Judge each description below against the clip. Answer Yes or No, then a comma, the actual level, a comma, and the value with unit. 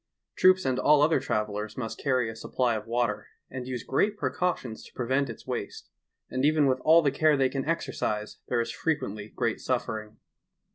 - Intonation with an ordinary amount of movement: Yes, average, 4.3 semitones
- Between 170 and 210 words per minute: Yes, average, 185 wpm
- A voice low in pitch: Yes, low, 130 Hz